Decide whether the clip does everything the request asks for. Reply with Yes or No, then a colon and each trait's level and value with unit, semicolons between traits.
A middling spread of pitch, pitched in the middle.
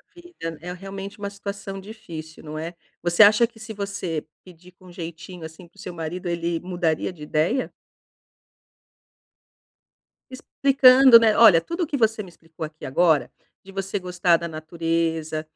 Yes: average, 3.8 semitones; medium, 180 Hz